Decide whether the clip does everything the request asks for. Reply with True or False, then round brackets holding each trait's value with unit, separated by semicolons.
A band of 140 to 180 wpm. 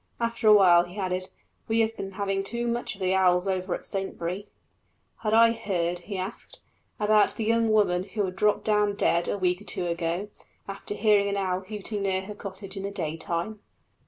False (200 wpm)